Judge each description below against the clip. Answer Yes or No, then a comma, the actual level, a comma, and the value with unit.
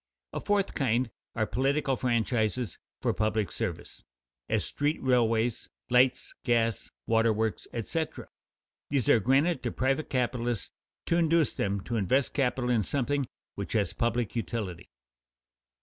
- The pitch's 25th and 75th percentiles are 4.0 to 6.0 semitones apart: No, average, 3.2 semitones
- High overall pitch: No, low, 120 Hz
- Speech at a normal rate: No, slow, 130 wpm